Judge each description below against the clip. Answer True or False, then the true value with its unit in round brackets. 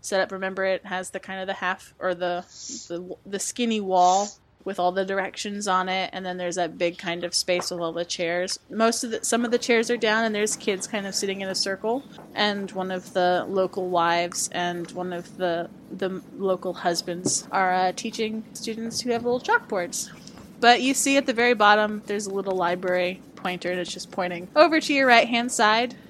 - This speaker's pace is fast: True (220 wpm)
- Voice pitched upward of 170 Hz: True (190 Hz)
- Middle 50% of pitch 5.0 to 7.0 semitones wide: False (4.0 semitones)